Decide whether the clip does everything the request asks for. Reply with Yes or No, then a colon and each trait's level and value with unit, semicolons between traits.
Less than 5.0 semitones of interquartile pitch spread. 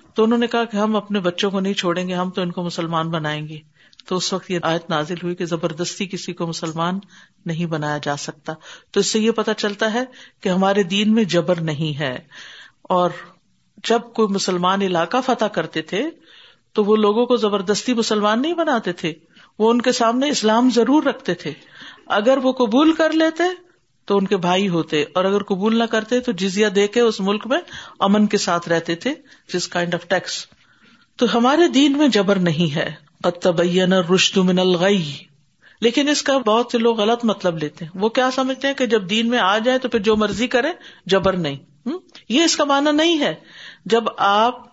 No: average, 5.3 semitones